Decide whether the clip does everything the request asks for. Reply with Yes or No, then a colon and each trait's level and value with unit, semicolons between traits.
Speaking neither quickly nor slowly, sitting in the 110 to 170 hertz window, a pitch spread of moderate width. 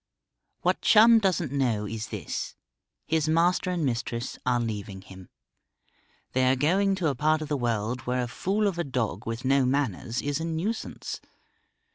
No: average, 170 wpm; low, 135 Hz; wide, 6.0 semitones